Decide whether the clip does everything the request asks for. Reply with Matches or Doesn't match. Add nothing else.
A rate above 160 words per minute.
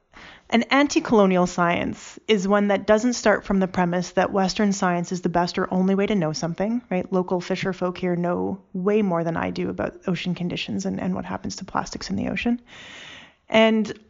Matches